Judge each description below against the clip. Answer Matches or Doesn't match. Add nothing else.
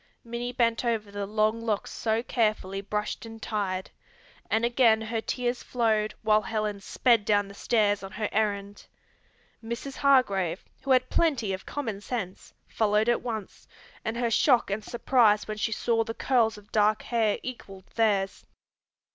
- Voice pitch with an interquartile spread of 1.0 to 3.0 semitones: Matches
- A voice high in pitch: Matches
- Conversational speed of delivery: Matches